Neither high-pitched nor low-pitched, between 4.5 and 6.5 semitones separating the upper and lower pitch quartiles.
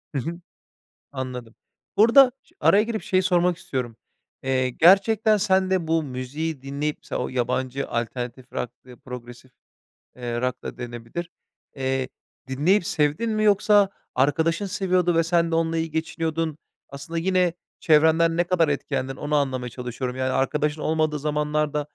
Yes: medium, 150 Hz; average, 5.1 semitones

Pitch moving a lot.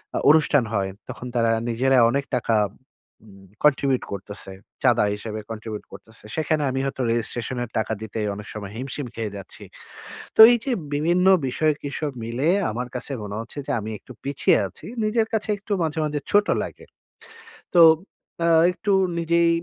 Yes: wide, 6.0 semitones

